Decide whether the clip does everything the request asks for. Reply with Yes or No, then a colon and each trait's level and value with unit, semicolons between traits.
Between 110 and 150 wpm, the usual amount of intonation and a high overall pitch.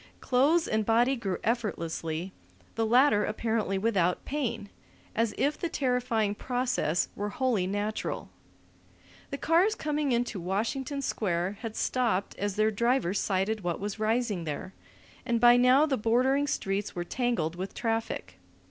Yes: average, 140 wpm; average, 4.2 semitones; high, 225 Hz